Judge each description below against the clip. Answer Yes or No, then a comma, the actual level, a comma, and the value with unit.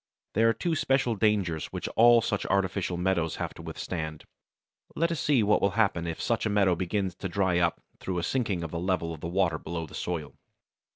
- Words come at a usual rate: No, fast, 215 wpm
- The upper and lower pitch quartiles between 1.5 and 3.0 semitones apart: No, average, 4.2 semitones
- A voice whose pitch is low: Yes, very low, 95 Hz